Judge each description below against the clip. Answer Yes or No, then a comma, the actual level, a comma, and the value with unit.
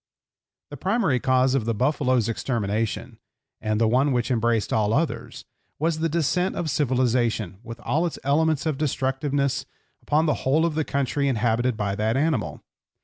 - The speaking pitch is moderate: No, low, 130 Hz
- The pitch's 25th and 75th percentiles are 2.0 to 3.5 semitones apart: No, average, 4.6 semitones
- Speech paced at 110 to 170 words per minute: Yes, average, 160 wpm